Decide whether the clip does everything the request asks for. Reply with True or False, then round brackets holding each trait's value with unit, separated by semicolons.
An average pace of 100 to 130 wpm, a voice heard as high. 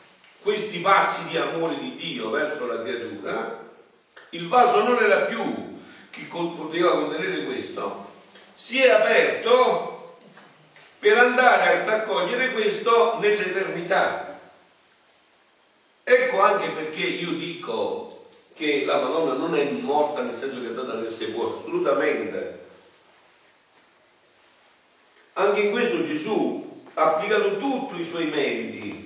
True (115 wpm; 250 Hz)